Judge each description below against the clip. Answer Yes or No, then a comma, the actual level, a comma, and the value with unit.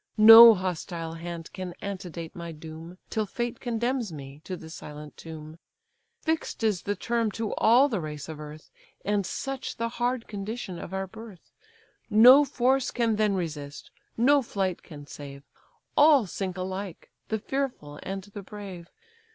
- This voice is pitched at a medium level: No, high, 195 Hz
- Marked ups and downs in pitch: Yes, wide, 5.7 semitones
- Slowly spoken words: No, average, 155 wpm